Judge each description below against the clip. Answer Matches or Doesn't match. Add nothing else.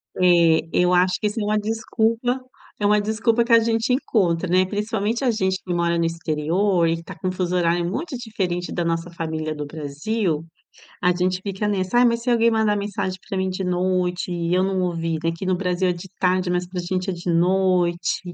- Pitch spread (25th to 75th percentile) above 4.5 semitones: Doesn't match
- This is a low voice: Doesn't match